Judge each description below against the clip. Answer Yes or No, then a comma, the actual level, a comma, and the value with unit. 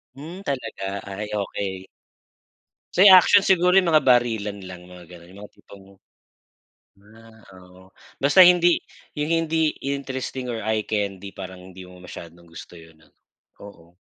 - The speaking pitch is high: No, low, 105 Hz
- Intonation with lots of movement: Yes, wide, 7.5 semitones